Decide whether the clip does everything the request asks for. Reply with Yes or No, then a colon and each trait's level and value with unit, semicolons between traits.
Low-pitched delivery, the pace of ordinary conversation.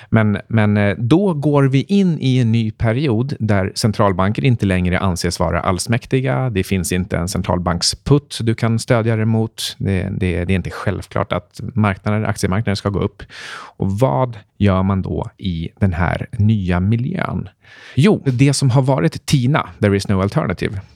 Yes: low, 105 Hz; average, 165 wpm